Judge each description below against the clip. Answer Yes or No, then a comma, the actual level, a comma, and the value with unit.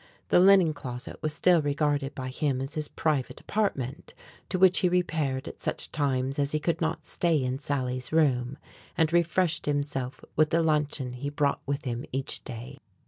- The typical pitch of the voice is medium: Yes, medium, 145 Hz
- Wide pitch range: No, average, 3.3 semitones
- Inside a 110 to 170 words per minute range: No, average, 180 wpm